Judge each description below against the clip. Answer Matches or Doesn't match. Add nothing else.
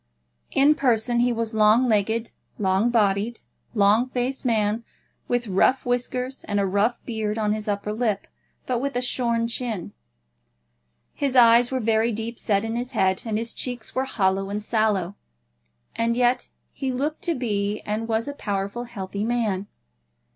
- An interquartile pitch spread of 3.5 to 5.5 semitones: Doesn't match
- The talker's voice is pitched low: Doesn't match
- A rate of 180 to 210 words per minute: Doesn't match